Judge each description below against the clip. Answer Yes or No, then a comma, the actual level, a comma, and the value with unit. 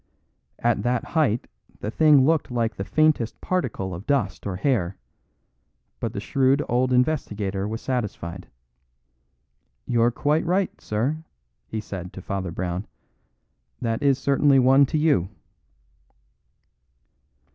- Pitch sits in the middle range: No, low, 120 Hz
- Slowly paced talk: Yes, slow, 125 wpm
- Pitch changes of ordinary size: No, wide, 5.8 semitones